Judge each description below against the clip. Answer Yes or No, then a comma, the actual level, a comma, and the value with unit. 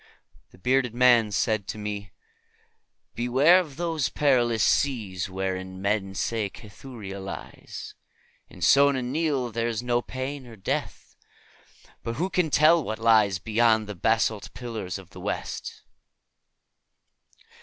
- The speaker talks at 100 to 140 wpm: Yes, slow, 135 wpm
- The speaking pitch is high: No, low, 115 Hz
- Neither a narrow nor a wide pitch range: Yes, average, 4.3 semitones